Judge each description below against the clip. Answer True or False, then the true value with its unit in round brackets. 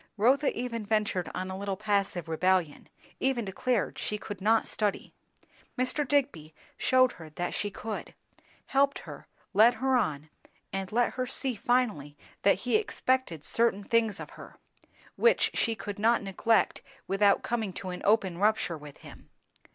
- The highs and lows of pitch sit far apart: False (4.4 semitones)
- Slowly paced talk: False (155 wpm)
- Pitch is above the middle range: True (210 Hz)